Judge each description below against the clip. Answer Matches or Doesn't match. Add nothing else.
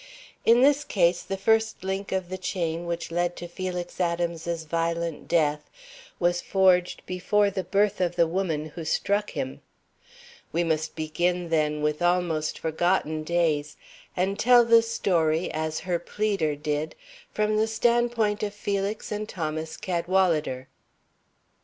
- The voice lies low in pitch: Doesn't match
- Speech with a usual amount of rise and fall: Matches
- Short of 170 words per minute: Matches